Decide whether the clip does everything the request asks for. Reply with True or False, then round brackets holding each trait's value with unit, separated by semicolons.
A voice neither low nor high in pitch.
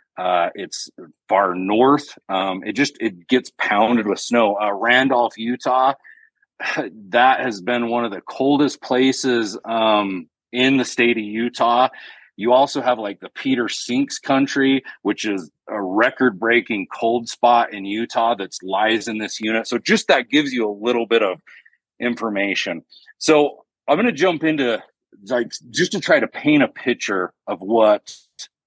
False (120 Hz)